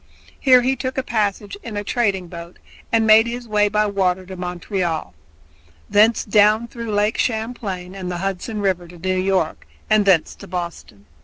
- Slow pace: No, average, 175 wpm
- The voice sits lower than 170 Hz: No, high, 200 Hz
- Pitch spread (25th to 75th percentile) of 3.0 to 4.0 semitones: Yes, average, 3.4 semitones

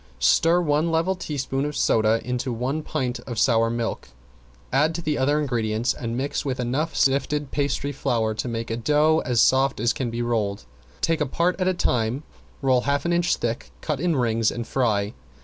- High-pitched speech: No, low, 130 Hz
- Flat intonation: No, average, 4.4 semitones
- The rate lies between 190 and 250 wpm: Yes, average, 195 wpm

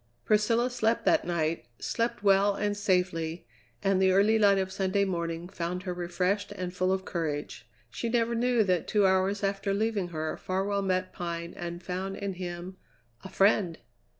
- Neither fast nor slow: Yes, average, 170 wpm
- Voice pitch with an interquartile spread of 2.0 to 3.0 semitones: Yes, narrow, 2.5 semitones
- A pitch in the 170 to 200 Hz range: Yes, high, 190 Hz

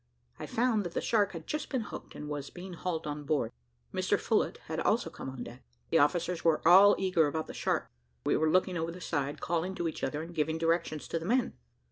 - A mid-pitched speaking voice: Yes, medium, 165 Hz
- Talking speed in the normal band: No, fast, 230 wpm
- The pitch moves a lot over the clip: No, average, 3.3 semitones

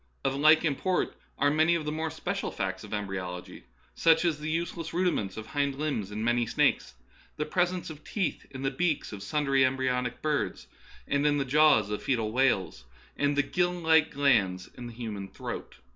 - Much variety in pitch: Yes, wide, 5.8 semitones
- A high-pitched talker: No, medium, 140 Hz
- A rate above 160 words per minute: Yes, average, 190 wpm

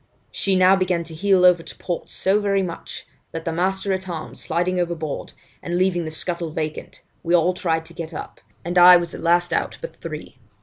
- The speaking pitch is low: No, medium, 175 Hz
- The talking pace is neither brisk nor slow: No, fast, 210 wpm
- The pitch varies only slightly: Yes, narrow, 1.9 semitones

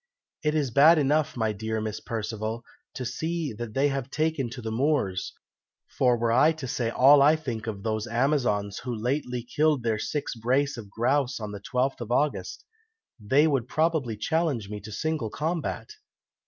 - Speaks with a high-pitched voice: No, low, 125 Hz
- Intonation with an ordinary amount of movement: Yes, average, 4.8 semitones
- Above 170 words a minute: Yes, average, 180 wpm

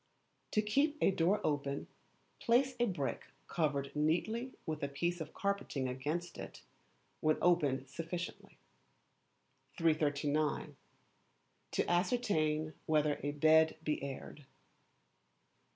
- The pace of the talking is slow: Yes, slow, 105 wpm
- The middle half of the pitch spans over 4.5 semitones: No, average, 3.6 semitones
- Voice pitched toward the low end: No, medium, 155 Hz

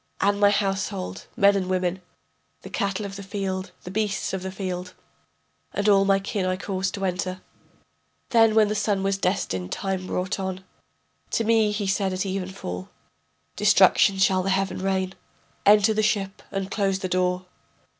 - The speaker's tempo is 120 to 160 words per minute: No, average, 175 wpm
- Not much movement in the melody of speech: Yes, narrow, 1.3 semitones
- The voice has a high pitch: Yes, high, 195 Hz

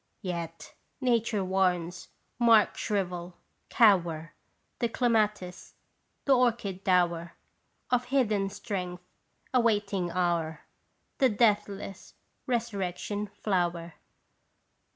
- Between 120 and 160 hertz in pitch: No, high, 195 Hz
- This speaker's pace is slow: Yes, slow, 80 wpm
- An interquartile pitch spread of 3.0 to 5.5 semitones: Yes, average, 4.2 semitones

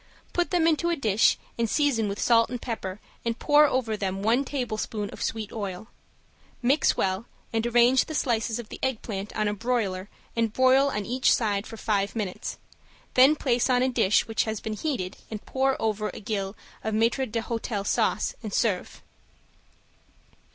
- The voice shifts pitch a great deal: No, average, 3.5 semitones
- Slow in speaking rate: No, average, 175 wpm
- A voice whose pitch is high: Yes, high, 225 Hz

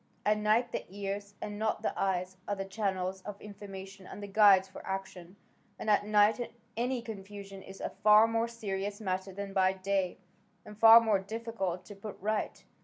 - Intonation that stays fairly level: Yes, narrow, 1.9 semitones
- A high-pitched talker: Yes, high, 200 Hz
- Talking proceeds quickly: No, average, 180 wpm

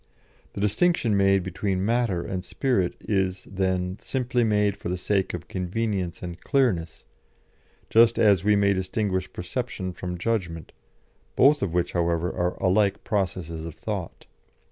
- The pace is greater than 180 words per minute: No, average, 145 wpm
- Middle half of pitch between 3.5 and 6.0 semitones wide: No, average, 3.1 semitones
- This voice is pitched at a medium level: No, very low, 95 Hz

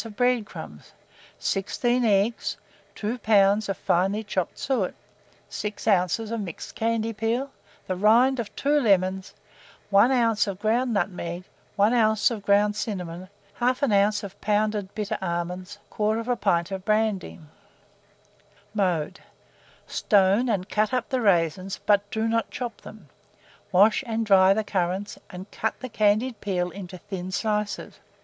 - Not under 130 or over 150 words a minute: Yes, average, 140 wpm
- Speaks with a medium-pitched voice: No, high, 205 Hz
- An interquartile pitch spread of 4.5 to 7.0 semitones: No, average, 2.9 semitones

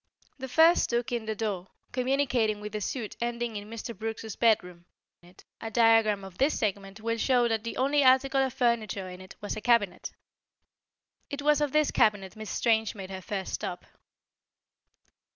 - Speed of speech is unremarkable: Yes, average, 170 wpm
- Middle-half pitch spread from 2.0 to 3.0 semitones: No, average, 3.4 semitones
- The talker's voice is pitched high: Yes, high, 225 Hz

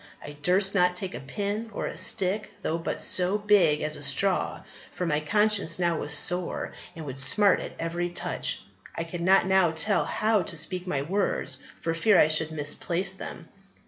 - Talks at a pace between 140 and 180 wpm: No, average, 190 wpm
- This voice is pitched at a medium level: Yes, medium, 180 Hz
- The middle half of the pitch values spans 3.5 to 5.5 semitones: Yes, average, 3.8 semitones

